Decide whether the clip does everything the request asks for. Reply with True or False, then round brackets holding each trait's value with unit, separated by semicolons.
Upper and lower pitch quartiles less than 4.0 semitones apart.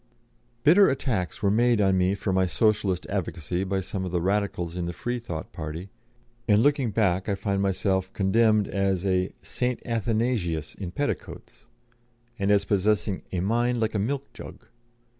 True (3.5 semitones)